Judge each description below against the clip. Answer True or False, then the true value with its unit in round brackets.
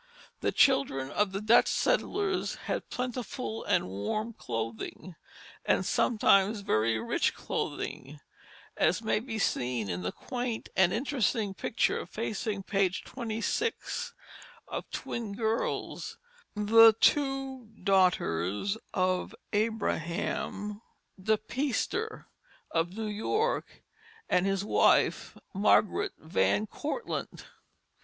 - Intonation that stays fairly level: False (4.6 semitones)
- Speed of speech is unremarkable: False (105 wpm)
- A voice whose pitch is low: False (210 Hz)